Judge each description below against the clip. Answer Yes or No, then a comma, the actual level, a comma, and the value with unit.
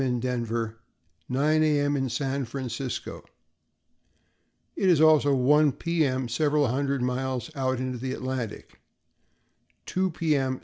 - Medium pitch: No, low, 130 Hz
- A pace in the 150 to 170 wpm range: No, average, 140 wpm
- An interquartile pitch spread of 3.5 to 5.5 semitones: No, average, 2.7 semitones